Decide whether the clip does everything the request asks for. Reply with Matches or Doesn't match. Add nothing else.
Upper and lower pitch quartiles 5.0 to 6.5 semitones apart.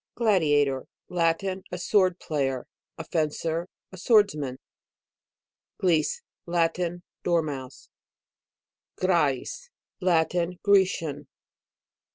Doesn't match